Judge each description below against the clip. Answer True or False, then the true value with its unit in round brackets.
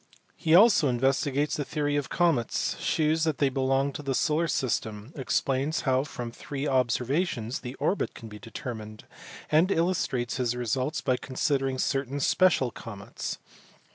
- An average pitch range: True (3.5 semitones)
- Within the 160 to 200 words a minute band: False (150 wpm)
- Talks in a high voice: False (135 Hz)